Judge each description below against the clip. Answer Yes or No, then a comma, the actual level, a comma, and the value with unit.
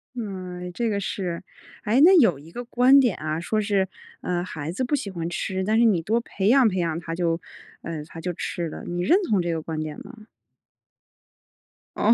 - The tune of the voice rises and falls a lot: No, average, 5.0 semitones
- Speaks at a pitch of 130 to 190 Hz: Yes, medium, 185 Hz